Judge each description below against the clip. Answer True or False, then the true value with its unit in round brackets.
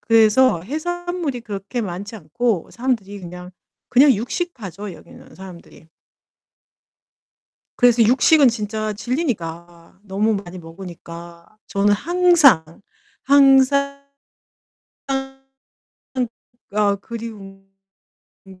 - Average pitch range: False (5.8 semitones)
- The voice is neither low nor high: False (215 Hz)